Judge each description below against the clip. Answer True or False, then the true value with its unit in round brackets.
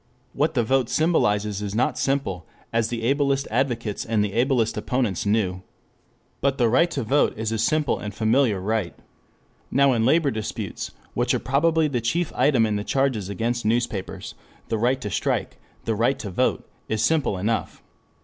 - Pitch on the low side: True (115 Hz)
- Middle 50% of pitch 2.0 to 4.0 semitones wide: False (4.4 semitones)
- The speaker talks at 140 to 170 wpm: False (180 wpm)